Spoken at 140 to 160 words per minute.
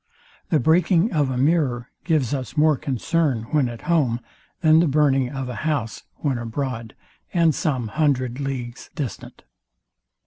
Yes: average, 145 wpm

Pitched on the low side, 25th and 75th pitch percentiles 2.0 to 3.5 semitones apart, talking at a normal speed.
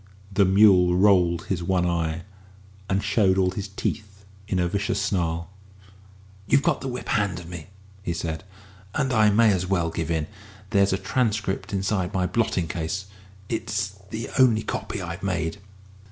Yes: very low, 95 Hz; average, 2.9 semitones; average, 165 wpm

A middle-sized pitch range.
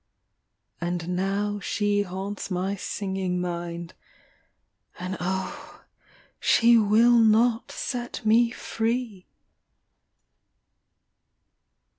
Yes: average, 4.0 semitones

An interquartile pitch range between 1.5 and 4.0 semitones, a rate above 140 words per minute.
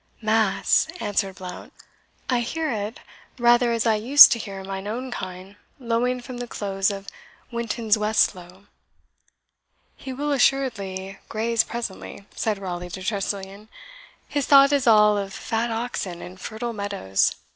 No: average, 3.6 semitones; slow, 135 wpm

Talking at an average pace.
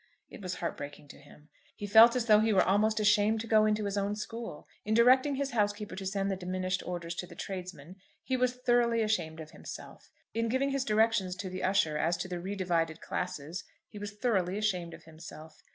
No: fast, 215 wpm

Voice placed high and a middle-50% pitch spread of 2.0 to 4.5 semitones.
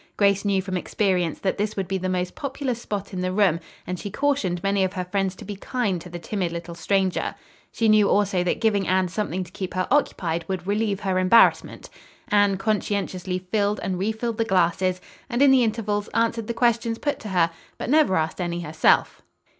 Yes: high, 195 Hz; average, 2.9 semitones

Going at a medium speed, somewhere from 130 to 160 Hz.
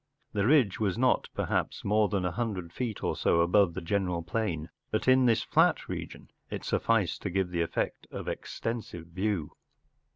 No: average, 175 wpm; low, 100 Hz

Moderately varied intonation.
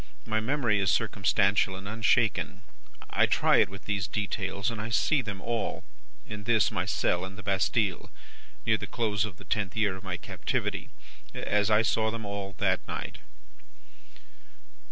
No: narrow, 2.2 semitones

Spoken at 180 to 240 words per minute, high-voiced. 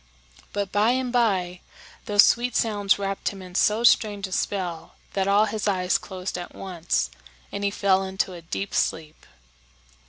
No: average, 165 wpm; high, 195 Hz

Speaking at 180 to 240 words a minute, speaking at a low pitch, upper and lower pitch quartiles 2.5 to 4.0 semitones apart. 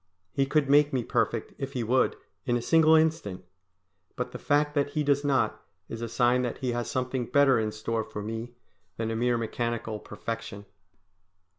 Yes: average, 185 wpm; low, 125 Hz; average, 3.7 semitones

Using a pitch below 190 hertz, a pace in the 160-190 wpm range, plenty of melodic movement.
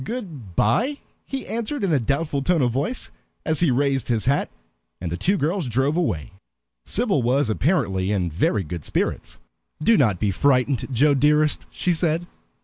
Yes: medium, 140 Hz; average, 170 wpm; wide, 7.0 semitones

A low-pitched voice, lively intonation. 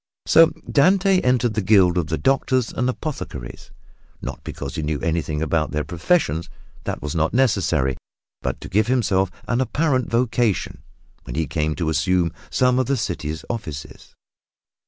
Yes: very low, 95 Hz; wide, 8.3 semitones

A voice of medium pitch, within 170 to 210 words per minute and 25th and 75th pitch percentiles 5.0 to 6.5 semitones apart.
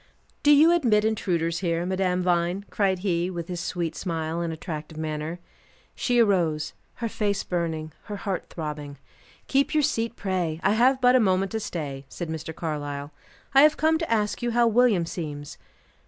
Yes: medium, 180 Hz; average, 175 wpm; wide, 5.5 semitones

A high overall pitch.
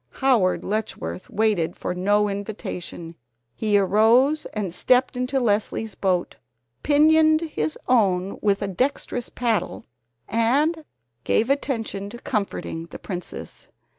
Yes: high, 215 Hz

